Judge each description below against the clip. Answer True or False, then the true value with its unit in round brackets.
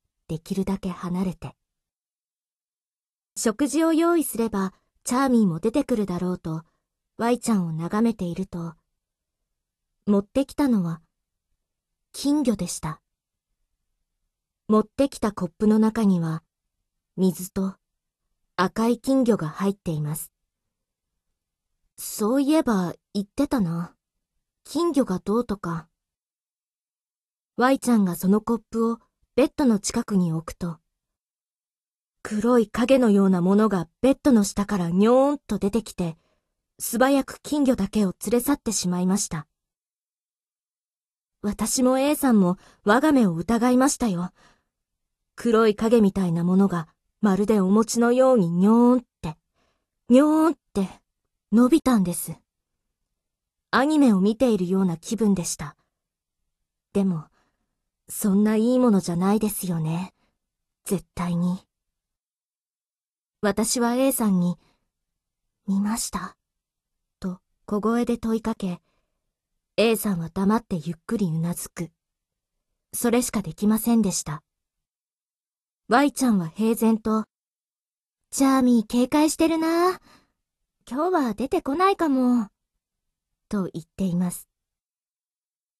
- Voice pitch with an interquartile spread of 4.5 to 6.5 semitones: True (5.6 semitones)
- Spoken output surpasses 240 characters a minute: False (235 characters per minute)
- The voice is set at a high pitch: True (205 Hz)